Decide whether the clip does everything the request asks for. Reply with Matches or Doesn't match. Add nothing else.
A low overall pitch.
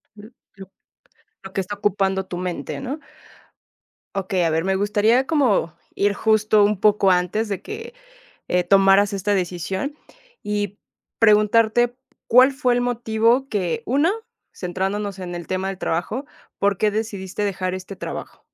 Doesn't match